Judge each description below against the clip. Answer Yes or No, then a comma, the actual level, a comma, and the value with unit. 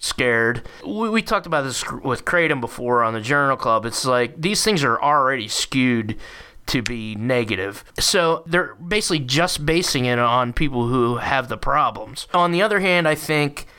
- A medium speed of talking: Yes, average, 180 wpm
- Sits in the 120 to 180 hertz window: Yes, medium, 140 Hz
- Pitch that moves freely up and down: Yes, wide, 6.1 semitones